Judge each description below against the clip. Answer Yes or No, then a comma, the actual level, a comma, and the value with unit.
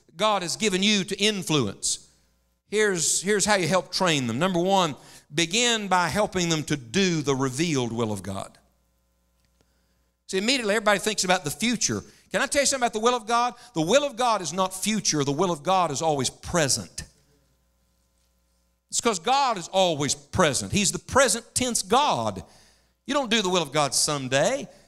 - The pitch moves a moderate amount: No, wide, 7.7 semitones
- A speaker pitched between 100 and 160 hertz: No, medium, 180 Hz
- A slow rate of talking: No, average, 185 wpm